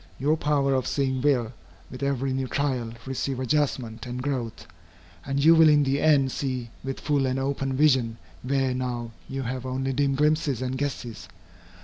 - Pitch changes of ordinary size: No, narrow, 1.9 semitones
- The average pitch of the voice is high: No, low, 135 Hz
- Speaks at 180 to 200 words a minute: No, average, 170 wpm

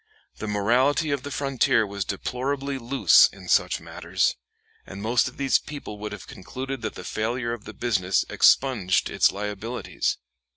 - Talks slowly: No, average, 160 wpm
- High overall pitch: No, low, 115 Hz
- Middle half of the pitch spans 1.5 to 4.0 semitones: No, average, 4.8 semitones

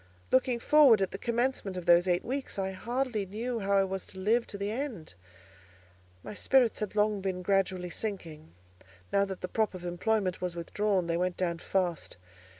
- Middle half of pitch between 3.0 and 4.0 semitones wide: Yes, average, 3.4 semitones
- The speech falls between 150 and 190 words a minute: Yes, average, 185 wpm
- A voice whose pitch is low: No, high, 195 Hz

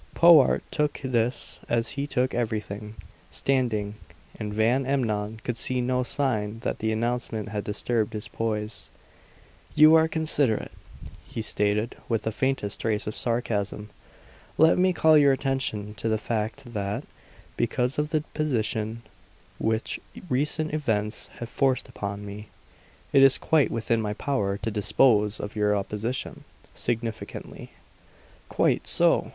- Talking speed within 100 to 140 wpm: Yes, slow, 135 wpm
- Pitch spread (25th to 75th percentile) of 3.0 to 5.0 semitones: Yes, average, 4.1 semitones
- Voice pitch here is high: No, low, 115 Hz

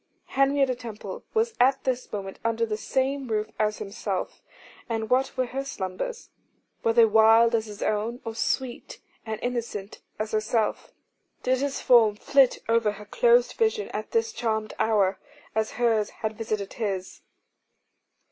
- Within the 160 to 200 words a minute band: No, average, 150 wpm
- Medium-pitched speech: No, high, 230 Hz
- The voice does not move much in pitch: No, average, 3.4 semitones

